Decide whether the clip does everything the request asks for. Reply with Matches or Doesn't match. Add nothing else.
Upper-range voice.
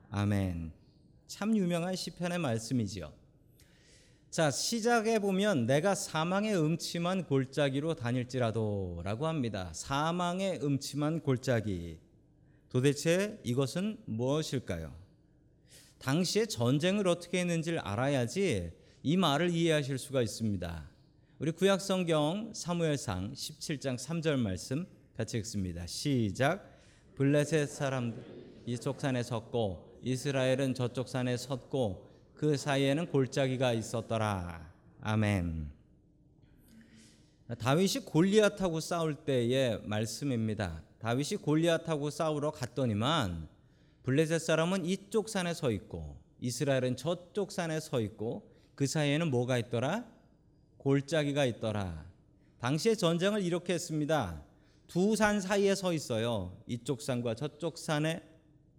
Doesn't match